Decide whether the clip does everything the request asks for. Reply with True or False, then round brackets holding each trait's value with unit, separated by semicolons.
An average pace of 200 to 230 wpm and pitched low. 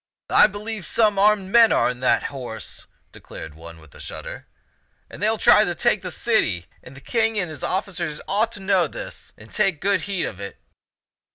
False (205 wpm; 190 Hz)